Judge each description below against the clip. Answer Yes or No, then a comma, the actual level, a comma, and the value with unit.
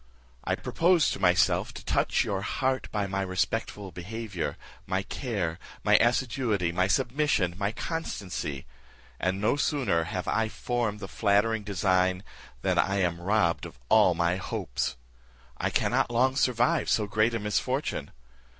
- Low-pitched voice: Yes, low, 100 Hz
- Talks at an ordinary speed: Yes, average, 145 wpm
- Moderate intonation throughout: Yes, average, 4.2 semitones